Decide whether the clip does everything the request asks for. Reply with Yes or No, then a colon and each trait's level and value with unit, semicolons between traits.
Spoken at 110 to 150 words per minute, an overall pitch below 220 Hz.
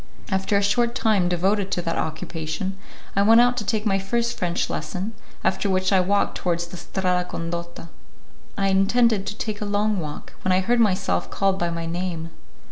No: average, 190 wpm; high, 190 Hz